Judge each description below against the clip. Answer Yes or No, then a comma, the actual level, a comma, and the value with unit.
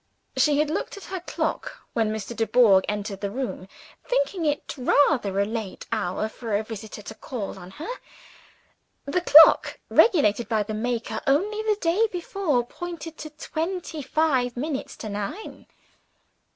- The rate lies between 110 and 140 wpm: No, average, 150 wpm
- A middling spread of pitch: No, wide, 7.3 semitones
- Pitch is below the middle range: No, very high, 255 Hz